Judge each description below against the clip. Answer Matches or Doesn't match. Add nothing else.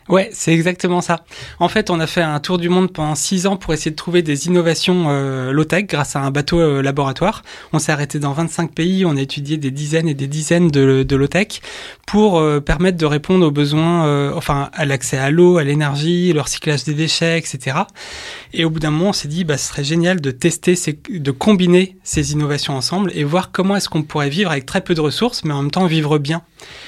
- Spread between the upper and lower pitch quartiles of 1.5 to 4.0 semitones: Matches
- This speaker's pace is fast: Matches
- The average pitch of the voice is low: Doesn't match